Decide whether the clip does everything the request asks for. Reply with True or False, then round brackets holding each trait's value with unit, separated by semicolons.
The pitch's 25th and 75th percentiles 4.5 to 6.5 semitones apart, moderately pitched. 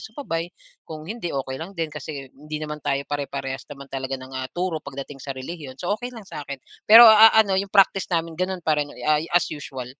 True (5.2 semitones; 155 Hz)